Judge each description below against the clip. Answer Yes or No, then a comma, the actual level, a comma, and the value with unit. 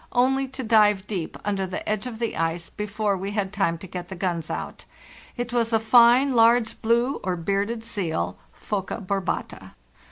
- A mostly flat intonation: No, average, 3.7 semitones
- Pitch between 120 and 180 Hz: No, high, 210 Hz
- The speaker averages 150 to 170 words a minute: No, average, 185 wpm